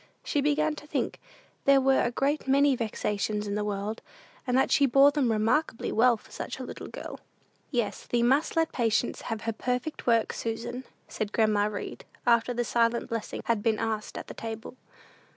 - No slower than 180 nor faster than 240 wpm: Yes, average, 190 wpm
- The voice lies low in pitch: No, high, 235 Hz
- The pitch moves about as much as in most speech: Yes, average, 3.6 semitones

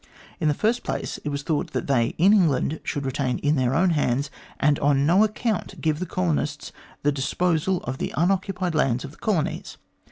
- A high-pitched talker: No, medium, 150 Hz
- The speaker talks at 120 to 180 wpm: No, average, 195 wpm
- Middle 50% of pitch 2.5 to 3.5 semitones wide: No, average, 4.4 semitones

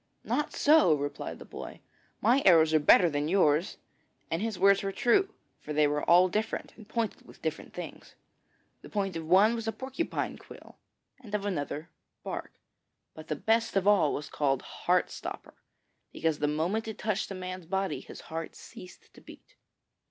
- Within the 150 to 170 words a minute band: No, average, 180 wpm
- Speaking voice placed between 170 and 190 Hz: Yes, medium, 185 Hz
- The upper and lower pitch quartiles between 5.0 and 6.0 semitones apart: Yes, wide, 5.6 semitones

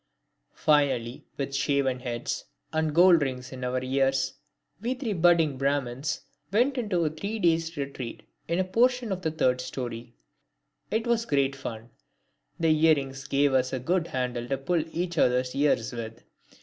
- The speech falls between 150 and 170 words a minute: Yes, average, 160 wpm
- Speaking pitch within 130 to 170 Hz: Yes, medium, 140 Hz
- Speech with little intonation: No, average, 5.0 semitones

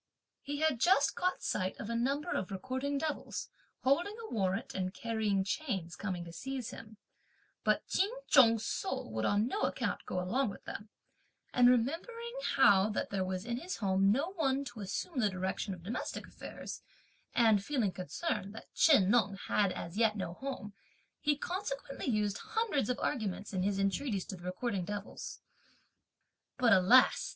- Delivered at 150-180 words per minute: Yes, average, 170 wpm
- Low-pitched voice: No, high, 220 Hz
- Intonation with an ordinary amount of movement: No, wide, 6.0 semitones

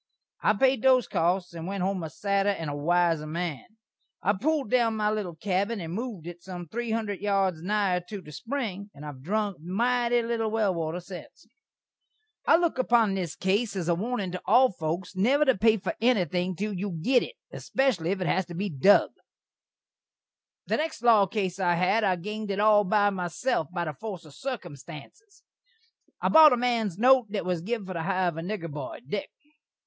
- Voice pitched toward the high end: Yes, high, 195 Hz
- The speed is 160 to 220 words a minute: Yes, average, 195 wpm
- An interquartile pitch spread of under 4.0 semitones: No, average, 4.3 semitones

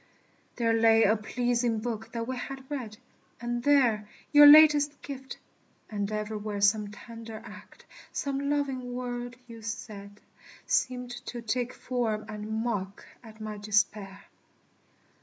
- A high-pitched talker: Yes, high, 230 Hz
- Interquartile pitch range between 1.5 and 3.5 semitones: Yes, average, 2.9 semitones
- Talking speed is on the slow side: Yes, slow, 130 wpm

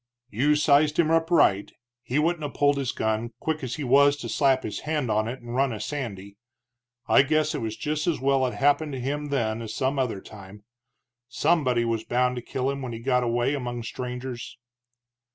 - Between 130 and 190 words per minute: No, fast, 205 wpm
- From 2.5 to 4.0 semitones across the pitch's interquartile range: Yes, average, 3.6 semitones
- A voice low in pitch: Yes, low, 130 Hz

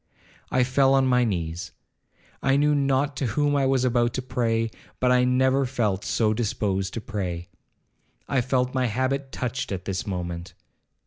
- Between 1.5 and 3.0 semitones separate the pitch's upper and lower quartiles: No, average, 4.3 semitones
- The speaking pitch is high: No, low, 125 Hz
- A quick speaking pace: No, average, 170 wpm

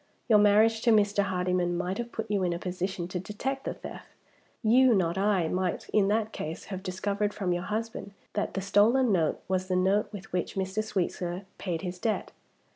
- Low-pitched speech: No, high, 195 Hz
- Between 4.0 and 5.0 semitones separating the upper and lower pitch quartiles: No, narrow, 2.6 semitones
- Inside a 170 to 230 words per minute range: Yes, average, 200 wpm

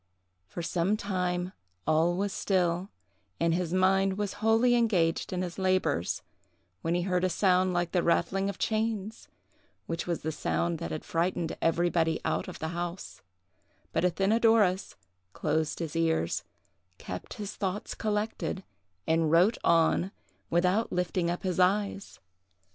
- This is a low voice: No, medium, 180 Hz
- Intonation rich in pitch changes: No, average, 2.7 semitones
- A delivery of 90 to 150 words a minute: Yes, average, 140 wpm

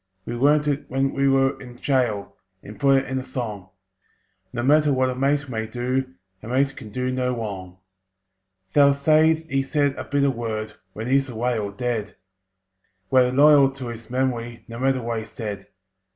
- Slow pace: No, average, 180 wpm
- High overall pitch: No, low, 130 Hz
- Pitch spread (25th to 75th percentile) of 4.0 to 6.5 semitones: No, average, 3.0 semitones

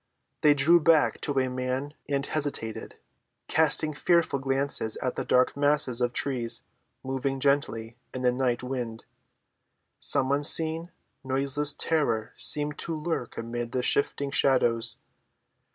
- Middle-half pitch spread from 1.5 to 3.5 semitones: Yes, average, 2.8 semitones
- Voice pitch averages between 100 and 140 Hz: Yes, low, 135 Hz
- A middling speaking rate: No, slow, 130 wpm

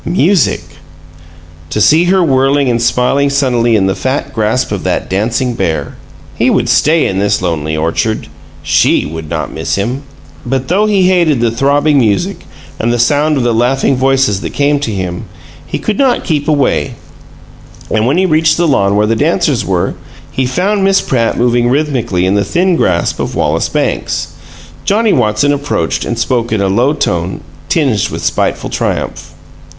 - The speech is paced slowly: No, average, 175 wpm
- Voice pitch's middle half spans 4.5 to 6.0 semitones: Yes, wide, 5.6 semitones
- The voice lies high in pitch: No, low, 125 Hz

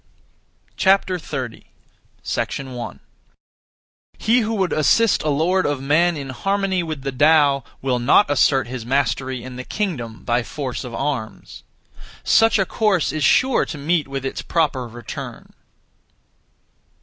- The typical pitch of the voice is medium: Yes, medium, 145 Hz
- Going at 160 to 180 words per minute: No, slow, 135 wpm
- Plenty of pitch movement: Yes, wide, 5.7 semitones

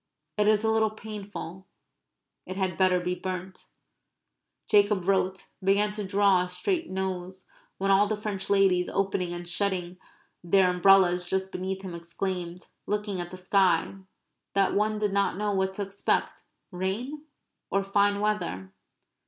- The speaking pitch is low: No, high, 190 Hz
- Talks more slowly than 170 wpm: Yes, average, 150 wpm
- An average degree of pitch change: No, narrow, 2.0 semitones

